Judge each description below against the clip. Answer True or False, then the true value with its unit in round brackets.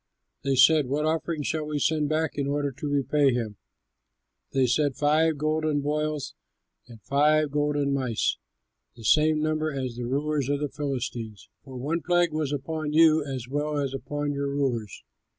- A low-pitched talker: False (145 Hz)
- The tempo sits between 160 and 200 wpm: True (170 wpm)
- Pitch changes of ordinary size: False (2.2 semitones)